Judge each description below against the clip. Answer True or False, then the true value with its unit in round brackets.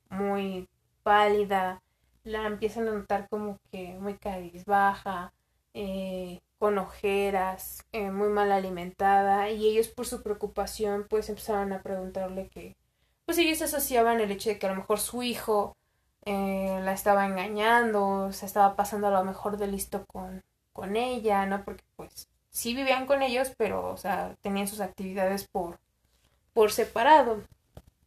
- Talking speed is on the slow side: False (150 wpm)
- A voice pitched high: True (200 Hz)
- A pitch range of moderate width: False (1.9 semitones)